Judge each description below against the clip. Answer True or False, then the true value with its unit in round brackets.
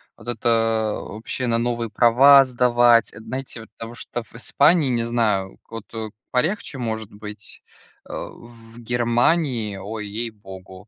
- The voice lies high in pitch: False (115 Hz)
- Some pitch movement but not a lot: False (1.8 semitones)